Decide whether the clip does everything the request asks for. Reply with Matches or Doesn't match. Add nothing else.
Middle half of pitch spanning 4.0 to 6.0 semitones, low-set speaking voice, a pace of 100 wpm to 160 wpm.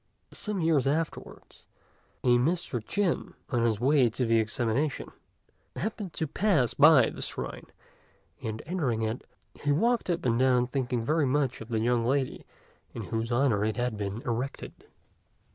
Matches